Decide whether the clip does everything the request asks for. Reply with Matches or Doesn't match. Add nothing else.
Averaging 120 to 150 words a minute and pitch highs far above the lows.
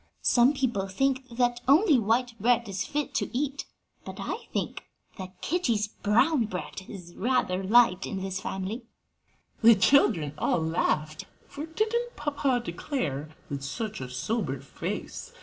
Matches